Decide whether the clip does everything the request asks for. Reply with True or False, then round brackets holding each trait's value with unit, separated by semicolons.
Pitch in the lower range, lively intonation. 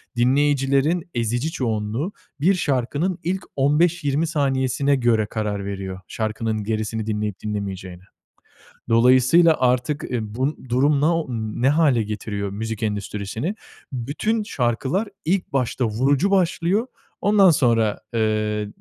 True (125 Hz; 5.9 semitones)